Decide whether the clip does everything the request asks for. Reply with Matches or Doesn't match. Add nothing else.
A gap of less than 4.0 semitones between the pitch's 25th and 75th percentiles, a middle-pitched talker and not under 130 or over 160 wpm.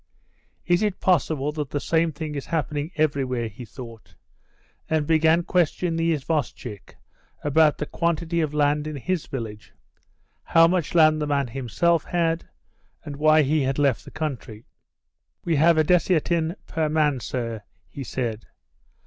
Matches